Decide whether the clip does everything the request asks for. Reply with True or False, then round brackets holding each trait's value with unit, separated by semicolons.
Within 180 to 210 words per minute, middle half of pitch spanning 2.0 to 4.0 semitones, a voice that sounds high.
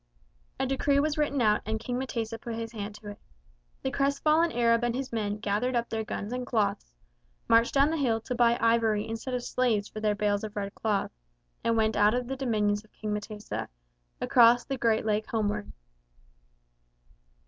True (190 wpm; 3.0 semitones; 225 Hz)